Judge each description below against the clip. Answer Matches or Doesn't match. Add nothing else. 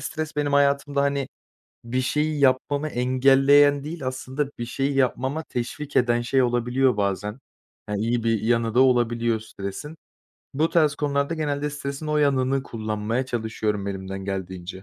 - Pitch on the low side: Matches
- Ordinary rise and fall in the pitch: Matches